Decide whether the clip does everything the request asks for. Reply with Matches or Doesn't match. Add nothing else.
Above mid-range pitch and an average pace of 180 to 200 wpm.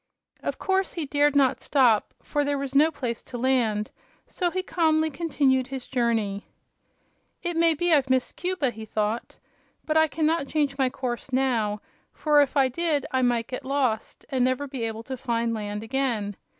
Matches